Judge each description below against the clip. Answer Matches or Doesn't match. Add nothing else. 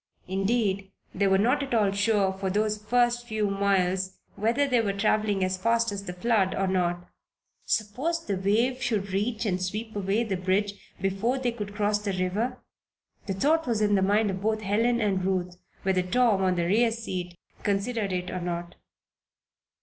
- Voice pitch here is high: Matches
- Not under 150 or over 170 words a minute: Doesn't match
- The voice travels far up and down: Doesn't match